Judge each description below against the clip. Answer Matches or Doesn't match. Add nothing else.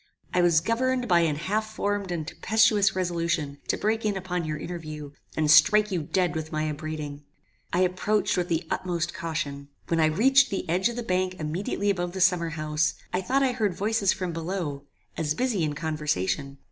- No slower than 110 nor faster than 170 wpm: Doesn't match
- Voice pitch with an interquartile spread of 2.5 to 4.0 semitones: Doesn't match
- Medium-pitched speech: Matches